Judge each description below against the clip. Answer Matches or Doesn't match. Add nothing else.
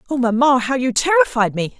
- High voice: Matches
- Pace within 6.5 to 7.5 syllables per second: Doesn't match